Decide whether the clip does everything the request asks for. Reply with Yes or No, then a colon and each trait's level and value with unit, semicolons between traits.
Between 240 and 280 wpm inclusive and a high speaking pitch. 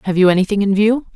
Yes: fast, 260 wpm; high, 200 Hz